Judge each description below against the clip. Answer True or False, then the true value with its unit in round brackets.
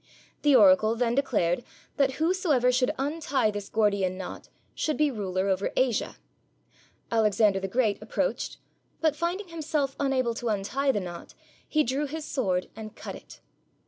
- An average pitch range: False (5.8 semitones)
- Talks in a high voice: True (250 Hz)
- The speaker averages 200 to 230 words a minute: False (150 wpm)